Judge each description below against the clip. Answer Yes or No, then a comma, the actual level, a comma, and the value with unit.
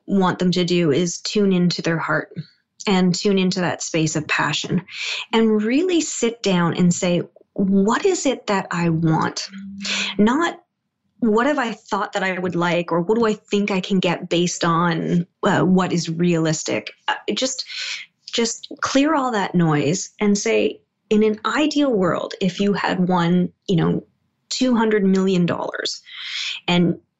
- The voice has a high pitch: Yes, high, 195 Hz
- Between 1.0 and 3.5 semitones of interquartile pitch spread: No, average, 4.4 semitones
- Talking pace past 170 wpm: No, average, 165 wpm